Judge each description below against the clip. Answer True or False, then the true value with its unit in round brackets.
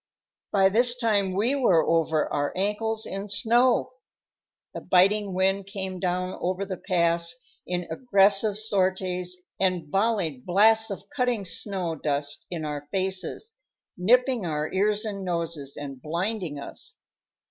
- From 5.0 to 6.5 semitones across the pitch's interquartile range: False (3.8 semitones)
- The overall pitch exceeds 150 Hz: True (190 Hz)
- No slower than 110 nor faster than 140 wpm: True (135 wpm)